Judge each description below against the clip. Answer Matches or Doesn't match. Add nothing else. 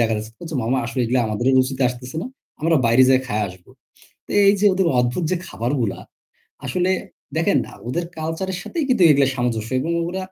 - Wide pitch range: Matches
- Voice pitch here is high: Doesn't match